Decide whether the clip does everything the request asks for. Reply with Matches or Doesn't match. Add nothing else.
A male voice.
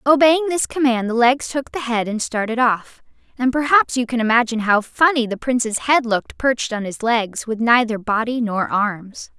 Doesn't match